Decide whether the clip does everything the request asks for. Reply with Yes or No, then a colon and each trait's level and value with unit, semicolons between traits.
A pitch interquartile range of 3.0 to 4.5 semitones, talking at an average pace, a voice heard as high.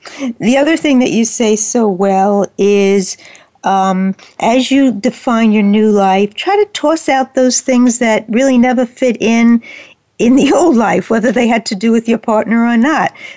Yes: average, 3.6 semitones; average, 185 wpm; high, 235 Hz